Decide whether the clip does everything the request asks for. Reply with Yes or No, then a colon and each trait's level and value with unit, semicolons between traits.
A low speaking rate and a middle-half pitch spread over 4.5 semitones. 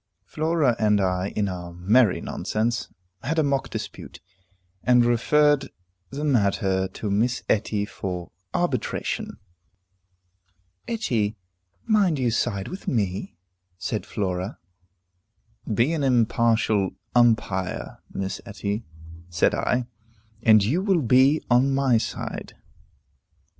Yes: slow, 110 wpm; average, 5.3 semitones